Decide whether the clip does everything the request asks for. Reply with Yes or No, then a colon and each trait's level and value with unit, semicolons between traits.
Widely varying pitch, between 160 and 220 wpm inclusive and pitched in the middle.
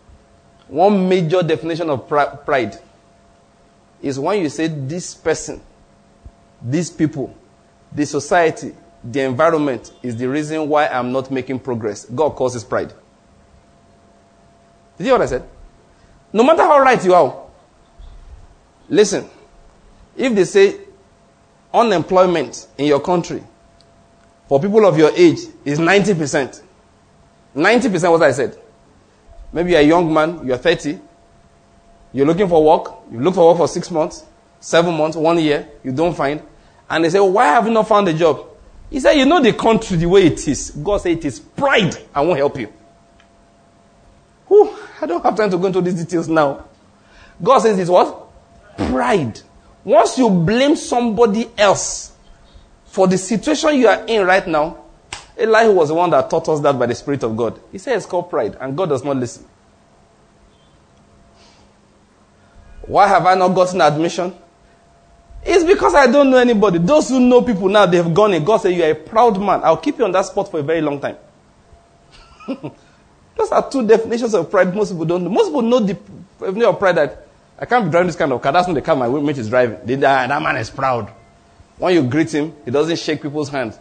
Yes: wide, 6.7 semitones; average, 185 wpm; medium, 165 Hz